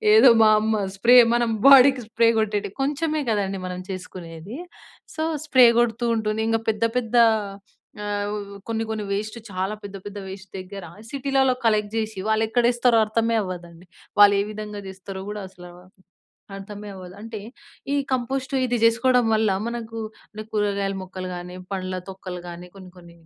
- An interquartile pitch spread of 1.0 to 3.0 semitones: No, average, 3.4 semitones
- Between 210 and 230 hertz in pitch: Yes, high, 215 Hz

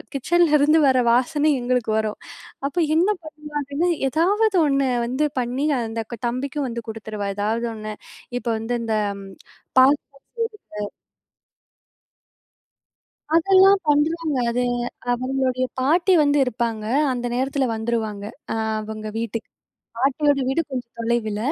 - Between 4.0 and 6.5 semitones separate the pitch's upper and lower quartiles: Yes, average, 4.5 semitones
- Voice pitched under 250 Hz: No, very high, 255 Hz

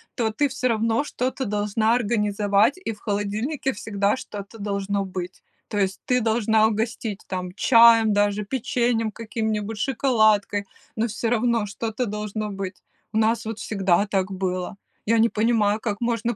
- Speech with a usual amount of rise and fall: No, narrow, 2.2 semitones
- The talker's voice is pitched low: No, high, 215 Hz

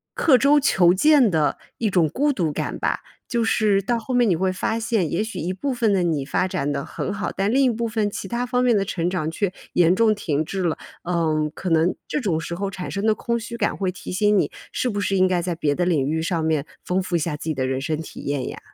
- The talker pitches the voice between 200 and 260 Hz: No, medium, 185 Hz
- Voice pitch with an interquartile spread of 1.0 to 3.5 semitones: No, average, 5.3 semitones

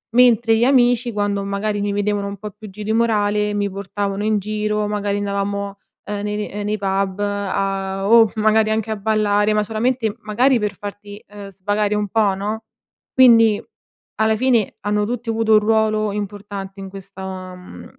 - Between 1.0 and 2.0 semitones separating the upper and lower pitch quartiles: Yes, narrow, 1.4 semitones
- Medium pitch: No, high, 210 Hz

